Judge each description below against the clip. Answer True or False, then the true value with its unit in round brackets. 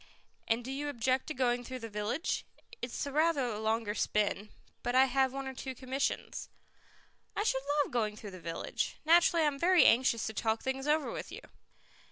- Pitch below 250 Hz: False (255 Hz)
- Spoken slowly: False (200 wpm)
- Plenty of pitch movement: False (3.8 semitones)